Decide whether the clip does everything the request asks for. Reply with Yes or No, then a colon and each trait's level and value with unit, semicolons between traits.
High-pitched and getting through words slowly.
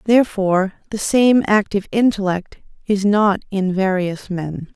Yes: high, 200 Hz; slow, 125 wpm